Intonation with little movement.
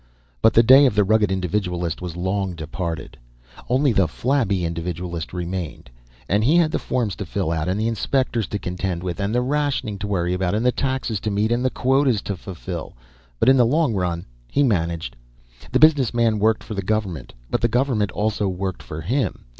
No: average, 5.1 semitones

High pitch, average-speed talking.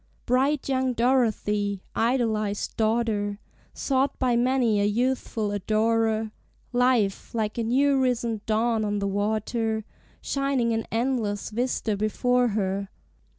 No: high, 225 Hz; slow, 115 wpm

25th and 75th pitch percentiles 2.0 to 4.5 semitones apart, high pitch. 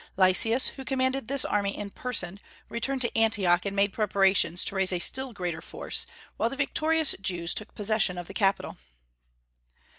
No: average, 5.2 semitones; high, 205 Hz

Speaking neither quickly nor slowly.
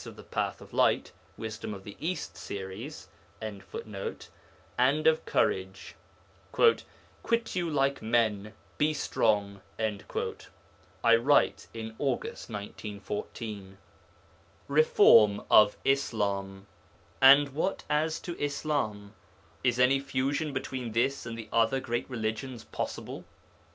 No: slow, 110 wpm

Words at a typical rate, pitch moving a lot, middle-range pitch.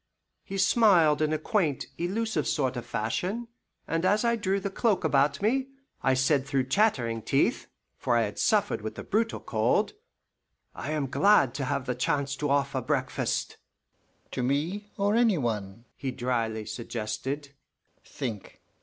Yes: average, 155 wpm; wide, 7.9 semitones; medium, 145 Hz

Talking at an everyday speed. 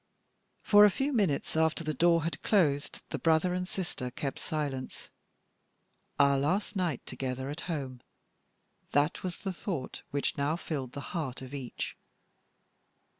Yes: average, 145 wpm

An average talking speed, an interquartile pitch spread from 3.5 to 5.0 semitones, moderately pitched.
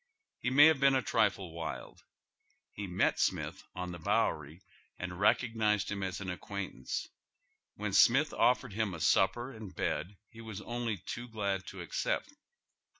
No: average, 160 wpm; average, 4.5 semitones; low, 100 Hz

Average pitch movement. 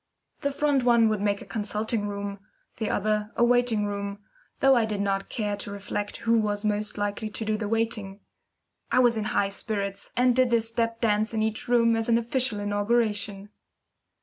No: narrow, 2.2 semitones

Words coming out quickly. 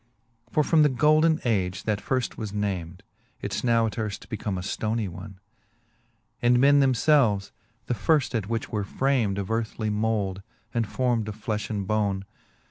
No: average, 165 wpm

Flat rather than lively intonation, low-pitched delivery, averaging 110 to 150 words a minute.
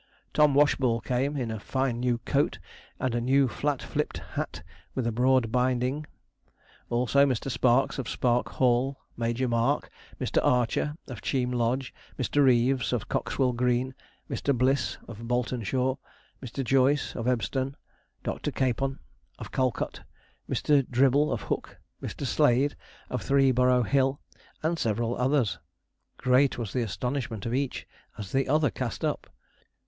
Yes: narrow, 2.1 semitones; low, 125 Hz; average, 145 wpm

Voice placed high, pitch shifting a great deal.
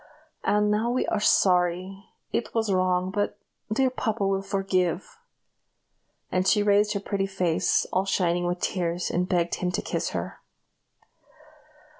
No: high, 195 Hz; narrow, 2.4 semitones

